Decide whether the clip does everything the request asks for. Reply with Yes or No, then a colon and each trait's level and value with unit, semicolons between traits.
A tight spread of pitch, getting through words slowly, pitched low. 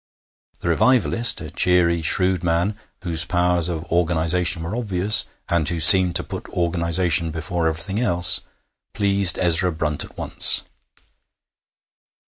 Yes: narrow, 1.9 semitones; slow, 125 wpm; very low, 85 Hz